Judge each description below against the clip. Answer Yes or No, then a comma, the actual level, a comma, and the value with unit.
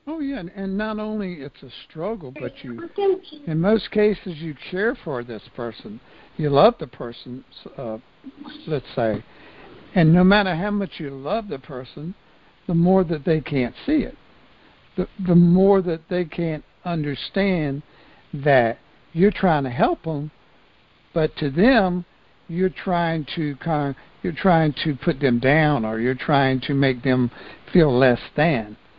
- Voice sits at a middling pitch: Yes, medium, 170 Hz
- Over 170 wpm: No, average, 160 wpm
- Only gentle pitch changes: No, wide, 5.5 semitones